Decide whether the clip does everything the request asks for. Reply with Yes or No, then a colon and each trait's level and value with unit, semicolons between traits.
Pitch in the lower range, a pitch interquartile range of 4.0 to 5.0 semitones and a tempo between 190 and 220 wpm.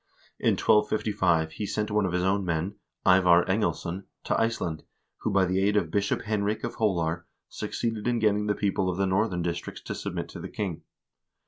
No: very low, 95 Hz; average, 3.1 semitones; average, 195 wpm